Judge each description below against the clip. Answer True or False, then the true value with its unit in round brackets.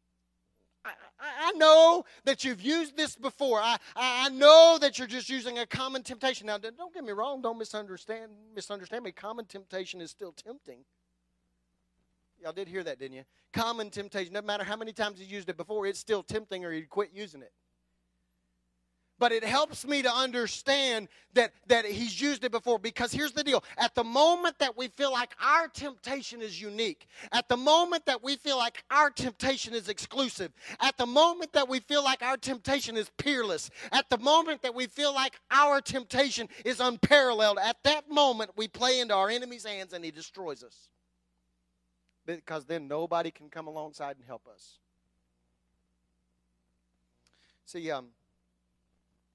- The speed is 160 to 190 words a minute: True (175 wpm)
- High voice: True (225 Hz)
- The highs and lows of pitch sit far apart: True (9.0 semitones)